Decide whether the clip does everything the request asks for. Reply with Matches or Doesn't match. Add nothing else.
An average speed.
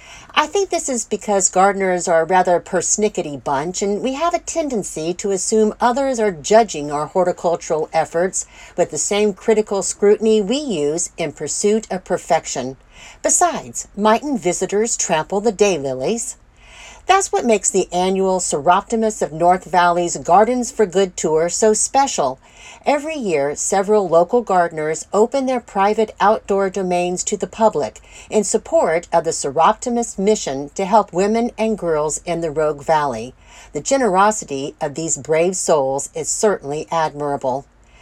Matches